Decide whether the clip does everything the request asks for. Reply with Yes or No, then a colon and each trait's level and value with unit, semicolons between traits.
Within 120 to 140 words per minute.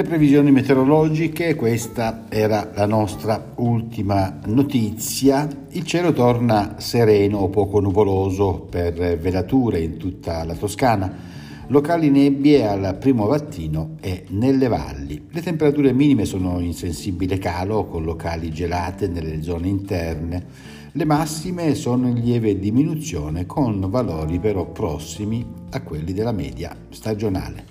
Yes: average, 125 wpm